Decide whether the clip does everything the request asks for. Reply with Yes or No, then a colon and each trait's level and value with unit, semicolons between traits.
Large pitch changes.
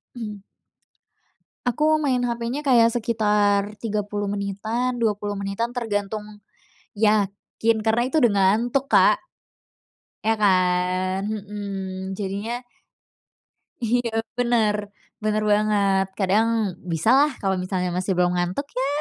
No: average, 2.9 semitones